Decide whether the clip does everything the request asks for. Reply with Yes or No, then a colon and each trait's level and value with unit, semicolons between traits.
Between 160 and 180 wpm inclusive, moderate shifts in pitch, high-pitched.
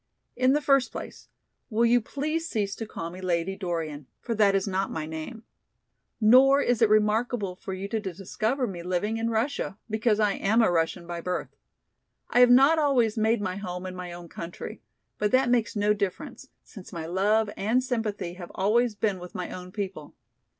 No: average, 190 wpm; average, 4.4 semitones; high, 210 Hz